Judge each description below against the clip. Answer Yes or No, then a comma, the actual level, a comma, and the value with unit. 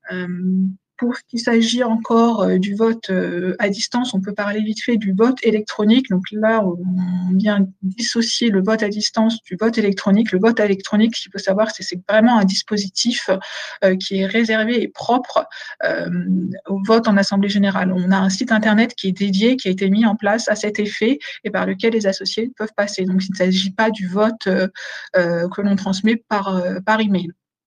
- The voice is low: No, high, 205 Hz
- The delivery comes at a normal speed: Yes, average, 195 wpm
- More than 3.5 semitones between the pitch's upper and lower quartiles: No, average, 2.9 semitones